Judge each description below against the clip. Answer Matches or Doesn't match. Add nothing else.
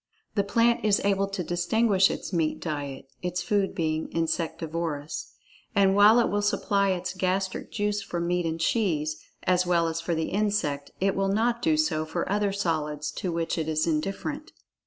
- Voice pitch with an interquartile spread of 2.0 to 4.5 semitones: Matches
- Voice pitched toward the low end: Doesn't match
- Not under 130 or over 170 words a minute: Doesn't match